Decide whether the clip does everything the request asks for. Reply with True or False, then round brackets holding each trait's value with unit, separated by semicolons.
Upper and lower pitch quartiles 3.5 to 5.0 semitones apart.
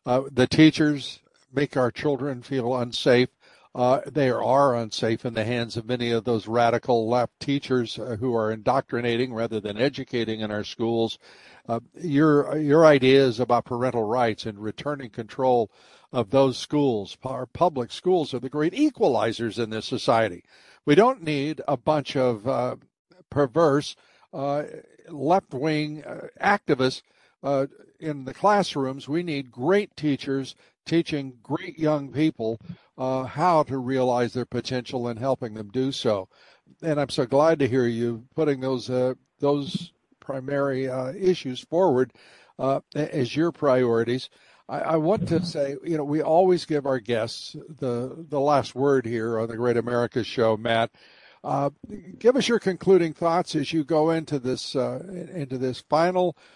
True (3.9 semitones)